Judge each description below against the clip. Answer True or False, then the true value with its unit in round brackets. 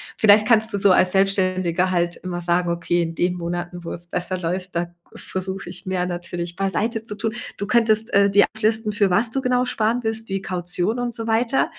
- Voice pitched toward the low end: False (195 Hz)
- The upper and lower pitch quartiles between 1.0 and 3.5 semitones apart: False (3.9 semitones)